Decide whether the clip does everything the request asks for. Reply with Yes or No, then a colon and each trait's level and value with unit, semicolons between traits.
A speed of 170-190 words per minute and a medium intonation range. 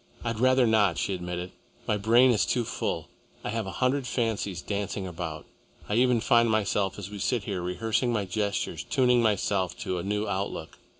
Yes: average, 185 wpm; average, 3.5 semitones